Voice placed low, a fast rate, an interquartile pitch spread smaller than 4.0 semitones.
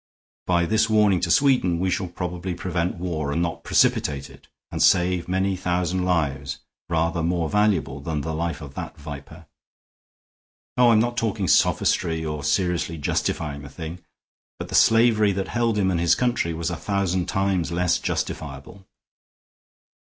No: very low, 90 Hz; average, 160 wpm; average, 3.1 semitones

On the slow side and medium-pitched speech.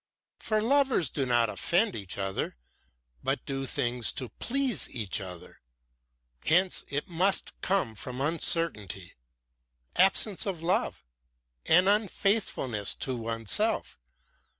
Yes: slow, 110 wpm; medium, 150 Hz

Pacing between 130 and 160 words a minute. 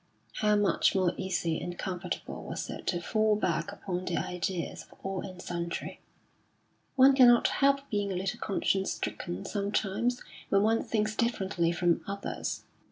Yes: average, 155 wpm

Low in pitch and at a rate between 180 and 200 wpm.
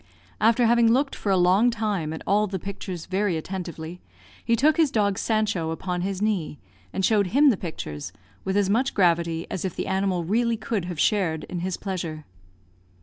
No: high, 190 Hz; average, 190 wpm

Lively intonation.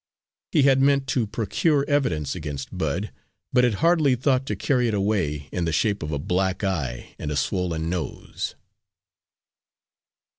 Yes: wide, 8.7 semitones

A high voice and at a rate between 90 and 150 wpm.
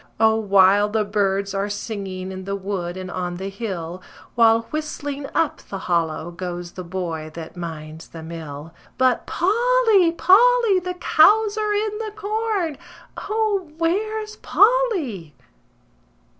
Yes: high, 215 Hz; slow, 135 wpm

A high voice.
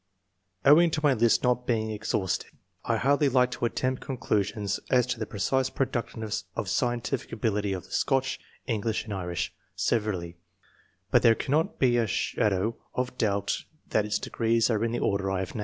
No: low, 115 Hz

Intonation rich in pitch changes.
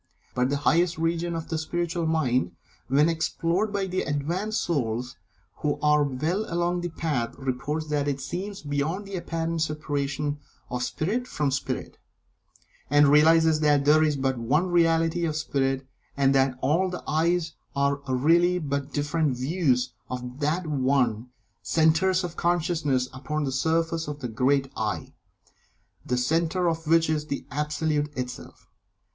No: average, 3.4 semitones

